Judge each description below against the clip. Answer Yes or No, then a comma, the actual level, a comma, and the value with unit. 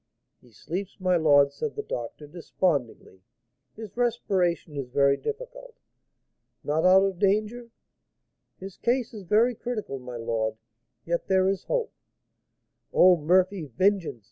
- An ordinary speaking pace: No, slow, 130 wpm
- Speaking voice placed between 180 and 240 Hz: Yes, medium, 185 Hz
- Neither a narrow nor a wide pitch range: No, wide, 7.0 semitones